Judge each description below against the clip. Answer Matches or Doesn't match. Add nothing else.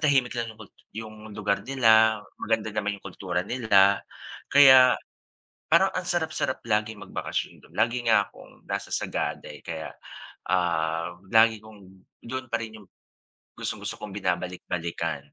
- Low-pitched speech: Matches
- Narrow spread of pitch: Doesn't match